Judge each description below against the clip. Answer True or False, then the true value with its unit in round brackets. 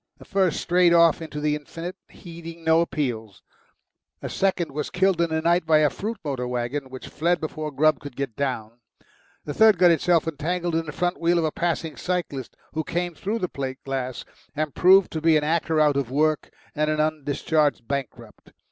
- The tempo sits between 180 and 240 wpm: True (195 wpm)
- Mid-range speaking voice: True (155 Hz)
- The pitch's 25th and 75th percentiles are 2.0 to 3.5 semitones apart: True (3.2 semitones)